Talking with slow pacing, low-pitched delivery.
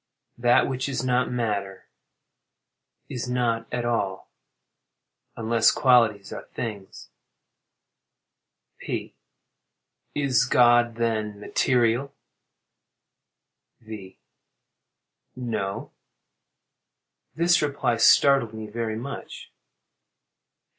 Yes: slow, 70 wpm; low, 120 Hz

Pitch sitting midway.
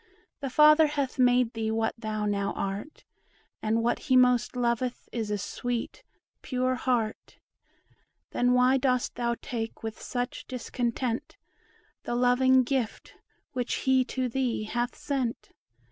No: high, 245 Hz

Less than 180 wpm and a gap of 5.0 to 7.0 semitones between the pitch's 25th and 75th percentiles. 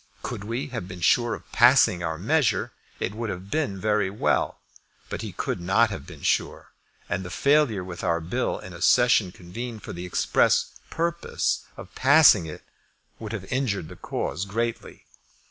Yes: average, 170 wpm; average, 5.3 semitones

